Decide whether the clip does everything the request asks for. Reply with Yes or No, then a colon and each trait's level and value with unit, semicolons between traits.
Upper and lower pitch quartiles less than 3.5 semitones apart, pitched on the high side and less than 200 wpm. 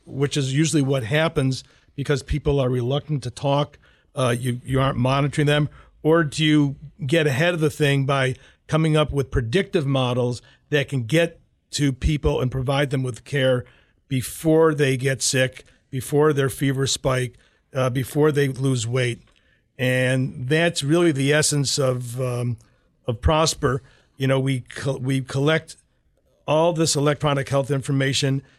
No: narrow, 2.4 semitones; medium, 140 Hz; average, 155 wpm